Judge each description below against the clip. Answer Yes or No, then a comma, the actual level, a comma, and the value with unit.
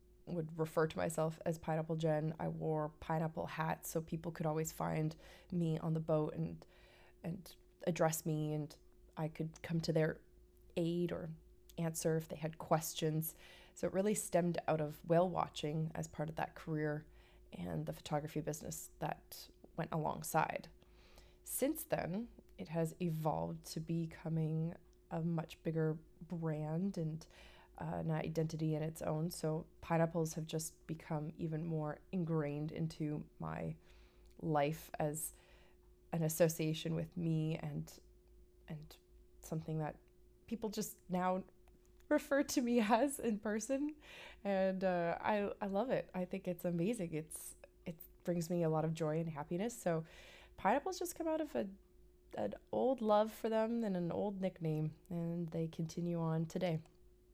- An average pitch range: No, narrow, 2.3 semitones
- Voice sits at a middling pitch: Yes, medium, 165 Hz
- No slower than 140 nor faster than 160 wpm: Yes, average, 150 wpm